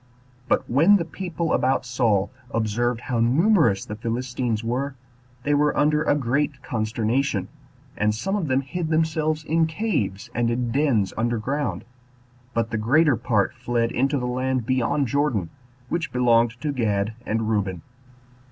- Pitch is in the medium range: No, low, 125 Hz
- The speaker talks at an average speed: Yes, average, 150 wpm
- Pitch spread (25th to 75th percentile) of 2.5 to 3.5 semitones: No, average, 4.5 semitones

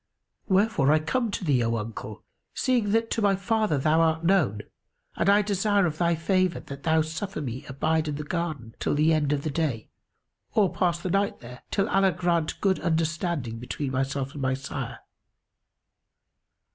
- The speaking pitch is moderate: Yes, medium, 160 Hz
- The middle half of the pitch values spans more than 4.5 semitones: Yes, wide, 5.6 semitones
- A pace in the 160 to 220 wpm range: Yes, average, 180 wpm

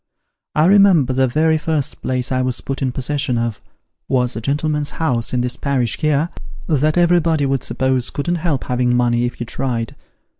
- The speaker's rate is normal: Yes, average, 180 wpm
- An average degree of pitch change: Yes, average, 3.8 semitones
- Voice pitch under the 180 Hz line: Yes, low, 135 Hz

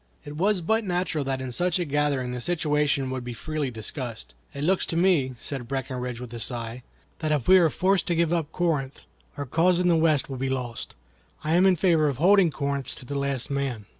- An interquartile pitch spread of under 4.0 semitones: No, average, 4.8 semitones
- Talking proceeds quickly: Yes, fast, 225 wpm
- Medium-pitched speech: Yes, medium, 145 Hz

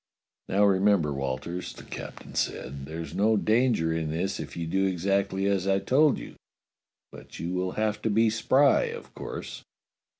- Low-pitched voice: Yes, very low, 95 Hz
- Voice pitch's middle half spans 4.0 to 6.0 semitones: Yes, average, 4.5 semitones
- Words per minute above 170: No, average, 165 wpm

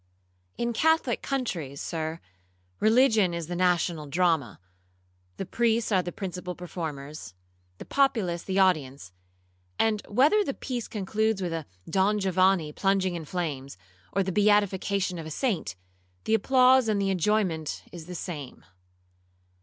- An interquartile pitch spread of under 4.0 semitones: No, average, 4.7 semitones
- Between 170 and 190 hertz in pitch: Yes, medium, 185 Hz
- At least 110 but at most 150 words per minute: Yes, average, 140 wpm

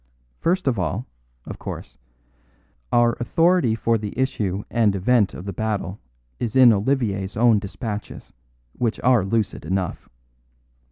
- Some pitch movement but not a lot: Yes, average, 3.6 semitones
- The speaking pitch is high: No, low, 110 Hz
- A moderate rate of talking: No, slow, 130 wpm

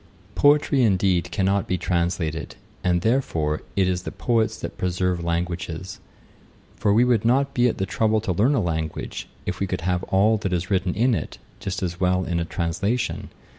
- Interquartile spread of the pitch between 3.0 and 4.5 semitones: Yes, average, 4.0 semitones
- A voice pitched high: No, very low, 95 Hz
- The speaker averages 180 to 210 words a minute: Yes, average, 185 wpm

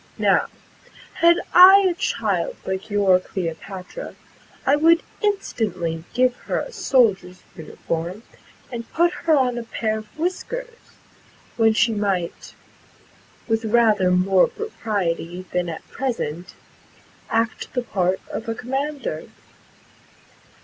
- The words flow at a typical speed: No, slow, 115 wpm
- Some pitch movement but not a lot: No, wide, 7.6 semitones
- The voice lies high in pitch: Yes, high, 225 Hz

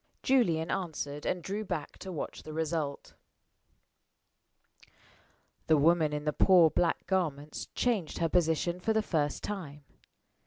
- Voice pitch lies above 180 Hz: No, medium, 165 Hz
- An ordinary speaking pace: No, slow, 130 wpm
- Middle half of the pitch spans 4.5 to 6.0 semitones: No, average, 3.5 semitones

